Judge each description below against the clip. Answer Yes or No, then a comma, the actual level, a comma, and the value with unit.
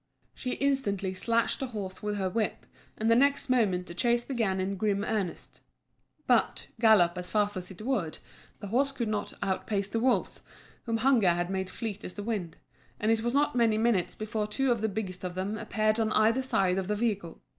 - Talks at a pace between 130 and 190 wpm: No, fast, 205 wpm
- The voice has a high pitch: Yes, high, 215 Hz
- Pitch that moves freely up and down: No, average, 3.6 semitones